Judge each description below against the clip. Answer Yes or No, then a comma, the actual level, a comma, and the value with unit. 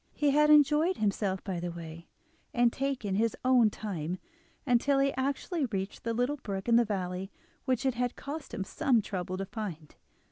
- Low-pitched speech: No, high, 230 Hz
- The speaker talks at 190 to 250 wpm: No, average, 180 wpm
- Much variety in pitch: Yes, wide, 6.0 semitones